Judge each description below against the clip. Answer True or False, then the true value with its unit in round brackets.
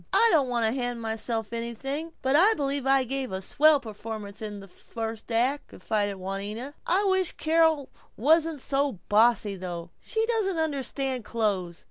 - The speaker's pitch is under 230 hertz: False (245 Hz)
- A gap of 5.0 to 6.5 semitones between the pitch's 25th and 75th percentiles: True (5.3 semitones)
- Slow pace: False (160 wpm)